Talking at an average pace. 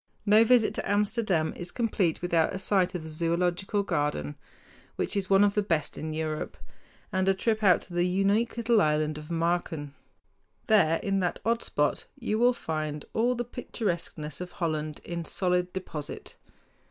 Yes: average, 170 wpm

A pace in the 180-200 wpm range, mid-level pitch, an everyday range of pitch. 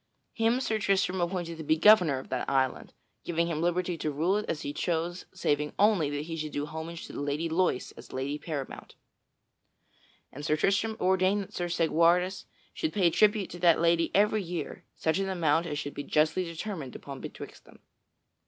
Yes: average, 190 wpm; medium, 170 Hz; average, 3.8 semitones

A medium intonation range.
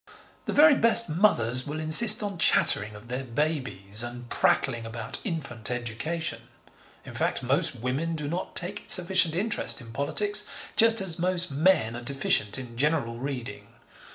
No: wide, 7.0 semitones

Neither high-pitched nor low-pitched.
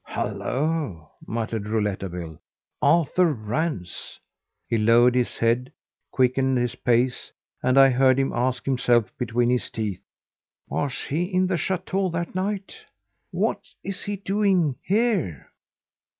No: low, 130 Hz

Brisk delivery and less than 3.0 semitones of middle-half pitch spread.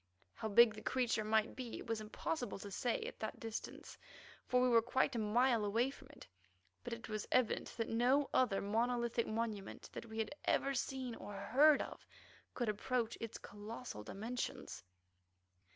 No: average, 170 wpm; narrow, 2.6 semitones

